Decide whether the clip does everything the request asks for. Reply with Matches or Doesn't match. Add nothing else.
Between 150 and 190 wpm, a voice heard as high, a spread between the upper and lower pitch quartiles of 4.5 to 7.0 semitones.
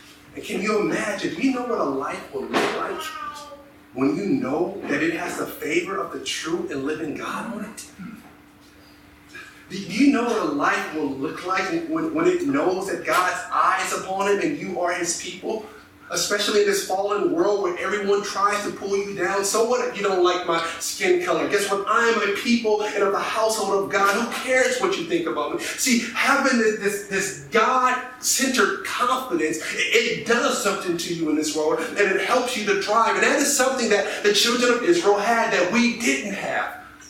Doesn't match